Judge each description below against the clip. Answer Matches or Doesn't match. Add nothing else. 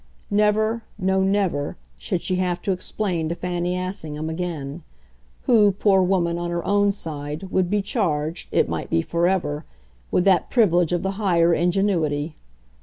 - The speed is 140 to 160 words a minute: Matches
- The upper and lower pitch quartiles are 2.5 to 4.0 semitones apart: Matches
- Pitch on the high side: Doesn't match